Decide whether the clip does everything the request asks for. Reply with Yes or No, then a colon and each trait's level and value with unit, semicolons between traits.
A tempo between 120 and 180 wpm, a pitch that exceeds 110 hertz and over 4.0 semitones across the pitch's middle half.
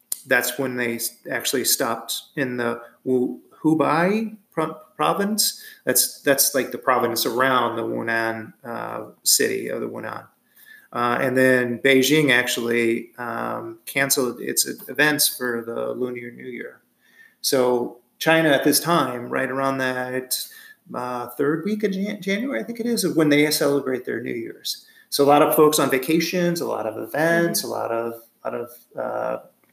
Yes: average, 160 wpm; low, 135 Hz; average, 5.2 semitones